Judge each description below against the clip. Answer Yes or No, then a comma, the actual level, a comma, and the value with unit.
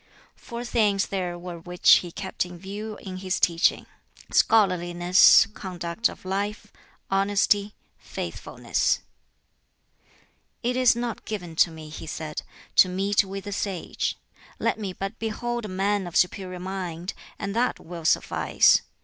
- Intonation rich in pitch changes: No, average, 2.8 semitones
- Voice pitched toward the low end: No, high, 195 Hz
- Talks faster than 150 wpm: No, average, 140 wpm